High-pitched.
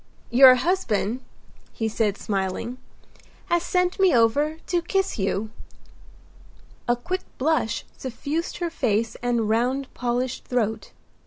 Yes: very high, 250 Hz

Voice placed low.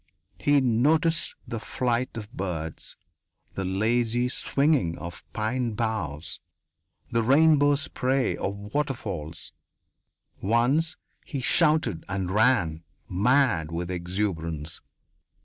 Yes: low, 115 Hz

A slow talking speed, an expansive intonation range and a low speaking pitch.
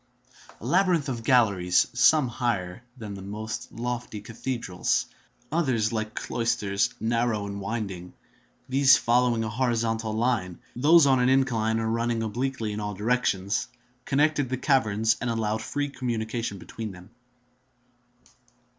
No: slow, 125 wpm; average, 2.8 semitones; low, 115 Hz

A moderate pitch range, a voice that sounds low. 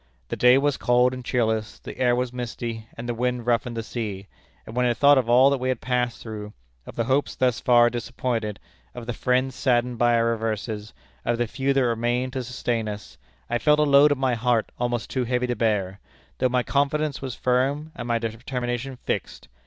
No: narrow, 1.9 semitones; low, 120 Hz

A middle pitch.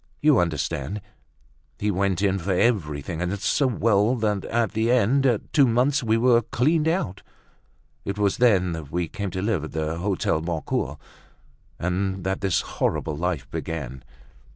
No: low, 100 Hz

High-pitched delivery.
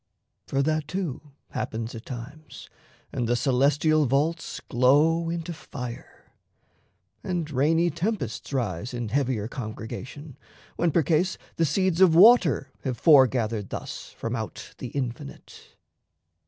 No: medium, 140 Hz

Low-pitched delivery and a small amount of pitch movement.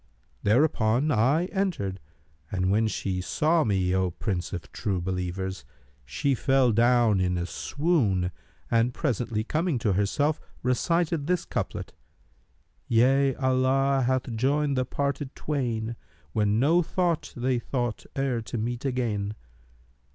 No: low, 120 Hz; wide, 5.4 semitones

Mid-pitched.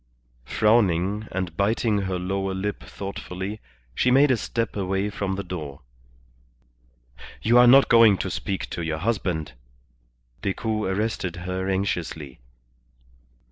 No: very low, 95 Hz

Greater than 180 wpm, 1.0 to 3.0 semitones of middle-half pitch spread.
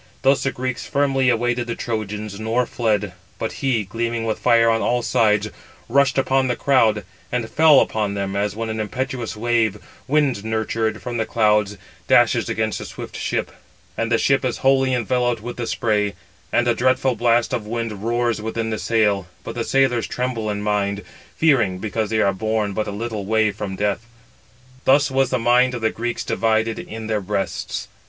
Yes: average, 190 wpm; narrow, 2.5 semitones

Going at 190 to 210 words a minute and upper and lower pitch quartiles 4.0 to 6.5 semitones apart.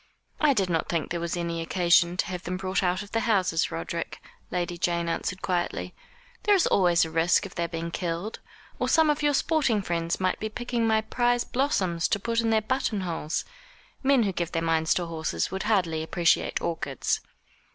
Yes: average, 200 wpm; average, 4.7 semitones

